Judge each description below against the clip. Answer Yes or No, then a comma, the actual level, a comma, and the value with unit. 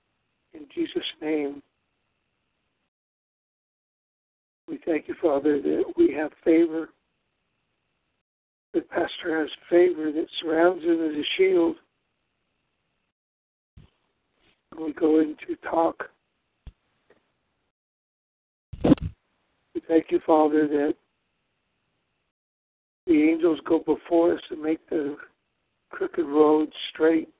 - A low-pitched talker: No, medium, 160 Hz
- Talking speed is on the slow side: Yes, slow, 90 wpm